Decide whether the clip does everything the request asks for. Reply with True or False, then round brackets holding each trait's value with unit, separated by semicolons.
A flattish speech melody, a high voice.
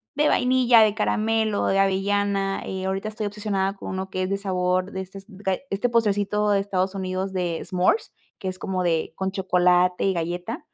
True (1.9 semitones; 195 Hz)